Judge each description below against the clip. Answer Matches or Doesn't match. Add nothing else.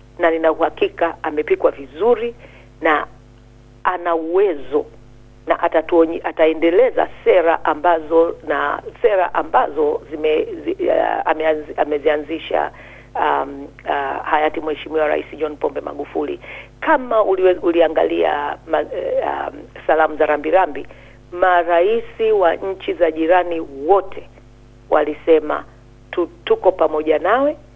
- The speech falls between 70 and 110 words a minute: Matches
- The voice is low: Doesn't match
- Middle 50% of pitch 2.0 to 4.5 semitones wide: Doesn't match